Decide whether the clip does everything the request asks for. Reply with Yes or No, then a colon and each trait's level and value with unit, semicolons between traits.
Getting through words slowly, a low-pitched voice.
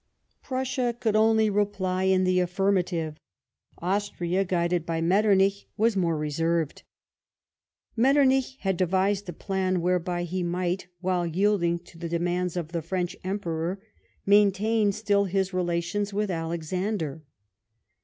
No: slow, 125 wpm; medium, 185 Hz